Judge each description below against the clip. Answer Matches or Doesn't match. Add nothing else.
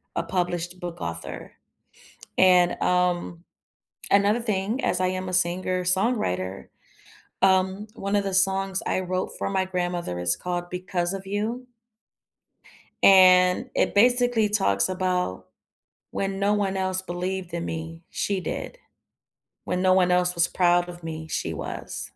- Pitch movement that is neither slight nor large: Doesn't match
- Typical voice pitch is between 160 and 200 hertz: Matches